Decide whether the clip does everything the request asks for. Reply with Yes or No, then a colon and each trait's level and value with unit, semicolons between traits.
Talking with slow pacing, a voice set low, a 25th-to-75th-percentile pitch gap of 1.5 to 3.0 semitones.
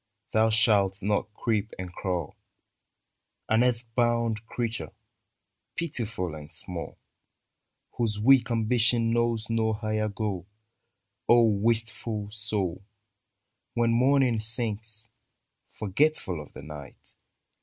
Yes: slow, 105 wpm; low, 110 Hz; narrow, 2.5 semitones